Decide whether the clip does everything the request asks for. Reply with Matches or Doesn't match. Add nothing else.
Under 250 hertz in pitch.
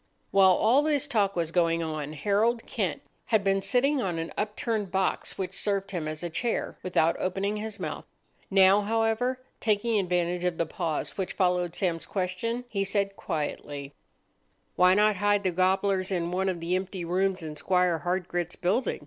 Matches